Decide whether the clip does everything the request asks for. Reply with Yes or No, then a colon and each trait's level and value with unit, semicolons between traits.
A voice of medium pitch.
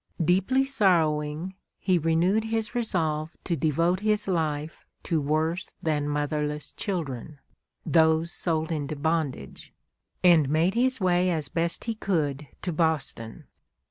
Yes: medium, 165 Hz